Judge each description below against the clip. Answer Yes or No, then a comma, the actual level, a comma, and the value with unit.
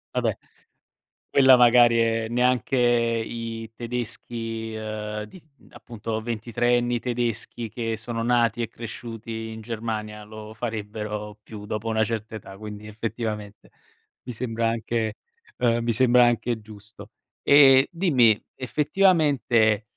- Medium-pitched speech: No, low, 115 Hz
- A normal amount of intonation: No, narrow, 1.8 semitones